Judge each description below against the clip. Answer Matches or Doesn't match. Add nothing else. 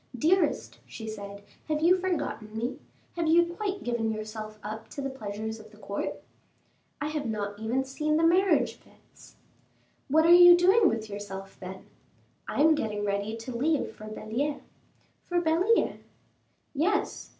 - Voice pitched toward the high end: Matches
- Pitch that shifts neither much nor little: Doesn't match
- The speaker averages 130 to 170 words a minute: Matches